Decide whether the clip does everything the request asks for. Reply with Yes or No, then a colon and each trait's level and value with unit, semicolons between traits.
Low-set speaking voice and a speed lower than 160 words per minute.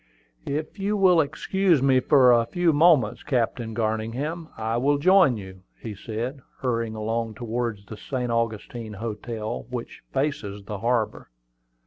Yes: low, 120 Hz; average, 140 wpm